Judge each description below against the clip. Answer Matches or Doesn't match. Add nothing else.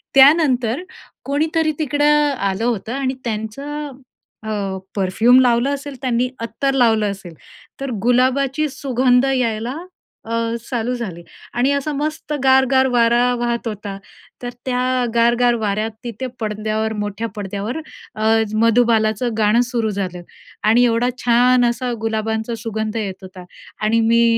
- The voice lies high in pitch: Matches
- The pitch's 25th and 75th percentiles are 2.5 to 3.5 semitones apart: Matches